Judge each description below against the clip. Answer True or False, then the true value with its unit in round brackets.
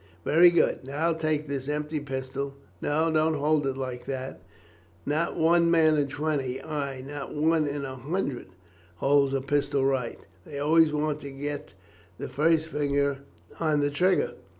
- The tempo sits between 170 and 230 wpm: False (160 wpm)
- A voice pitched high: False (145 Hz)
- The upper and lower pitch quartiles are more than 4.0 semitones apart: False (2.4 semitones)